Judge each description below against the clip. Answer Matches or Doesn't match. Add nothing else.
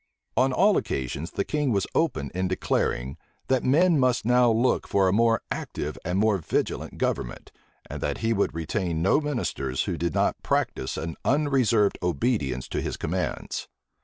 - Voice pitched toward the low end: Matches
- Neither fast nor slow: Matches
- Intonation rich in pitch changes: Matches